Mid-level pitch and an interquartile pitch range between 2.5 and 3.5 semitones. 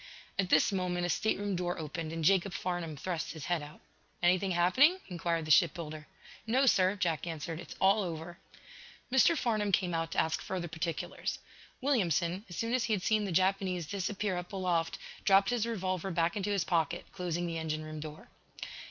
Yes: medium, 180 Hz; average, 3.1 semitones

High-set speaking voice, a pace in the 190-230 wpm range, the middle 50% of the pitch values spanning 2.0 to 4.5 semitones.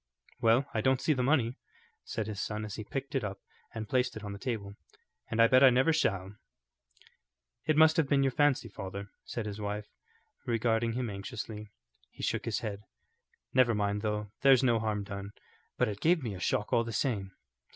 No: low, 110 Hz; average, 200 wpm; average, 3.8 semitones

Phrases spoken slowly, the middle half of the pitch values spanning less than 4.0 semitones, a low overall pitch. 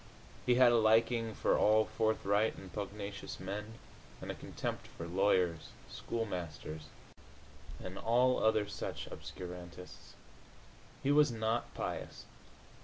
Yes: slow, 115 wpm; average, 3.6 semitones; low, 105 Hz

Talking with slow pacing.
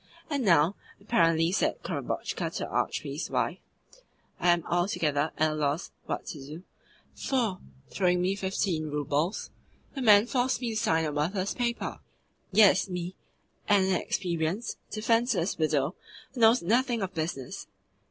No: average, 145 wpm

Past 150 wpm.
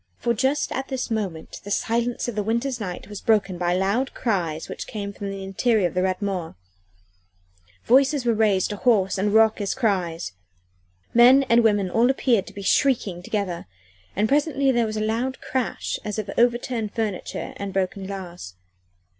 Yes: average, 175 wpm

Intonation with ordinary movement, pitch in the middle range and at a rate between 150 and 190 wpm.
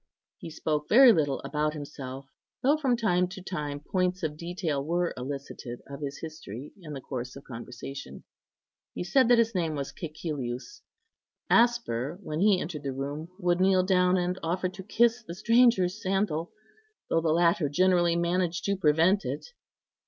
Yes: average, 4.4 semitones; medium, 170 Hz; average, 165 wpm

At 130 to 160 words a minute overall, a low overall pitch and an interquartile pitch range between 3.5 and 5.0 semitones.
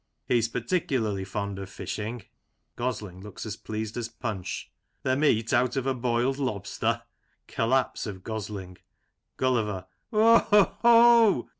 Yes: average, 140 wpm; low, 115 Hz; average, 4.0 semitones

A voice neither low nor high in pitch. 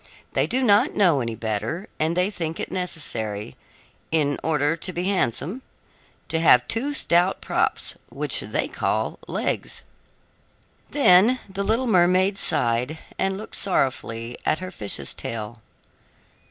Yes: medium, 170 Hz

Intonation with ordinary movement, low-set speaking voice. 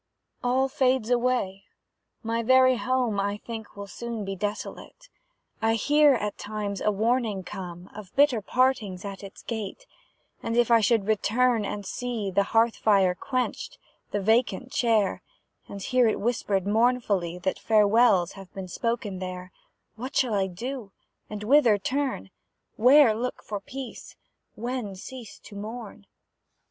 No: average, 3.7 semitones; high, 220 Hz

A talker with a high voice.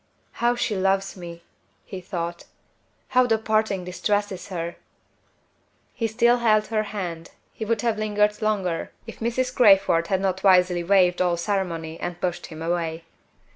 Yes: high, 195 Hz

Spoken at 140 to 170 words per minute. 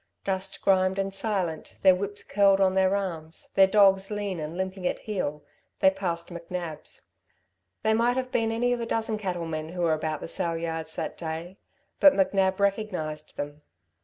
No: average, 180 wpm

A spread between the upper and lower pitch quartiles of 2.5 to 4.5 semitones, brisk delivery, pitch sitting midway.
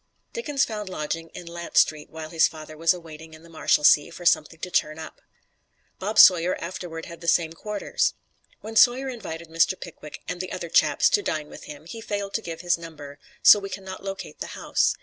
Yes: average, 3.3 semitones; fast, 210 wpm; medium, 170 Hz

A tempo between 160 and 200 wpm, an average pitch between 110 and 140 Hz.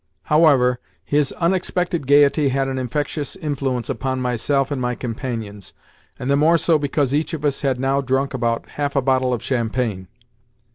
Yes: average, 165 wpm; low, 135 Hz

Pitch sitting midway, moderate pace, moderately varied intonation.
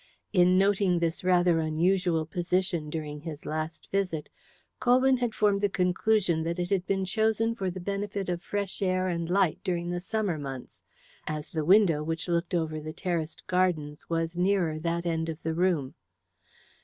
Yes: medium, 175 Hz; average, 170 wpm; average, 3.0 semitones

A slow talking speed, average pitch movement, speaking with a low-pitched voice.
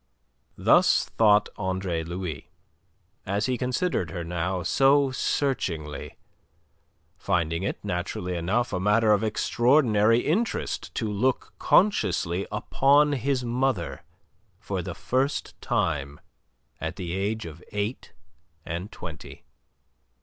No: slow, 110 wpm; wide, 6.3 semitones; low, 105 Hz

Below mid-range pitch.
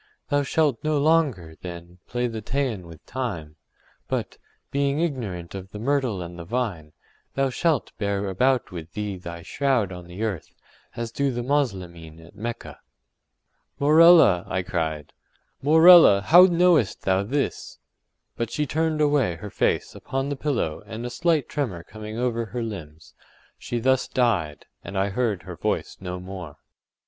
Yes: low, 115 Hz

